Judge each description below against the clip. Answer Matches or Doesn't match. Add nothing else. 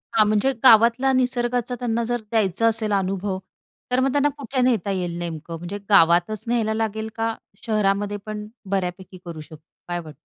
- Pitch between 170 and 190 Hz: Doesn't match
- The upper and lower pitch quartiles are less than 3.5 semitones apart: Doesn't match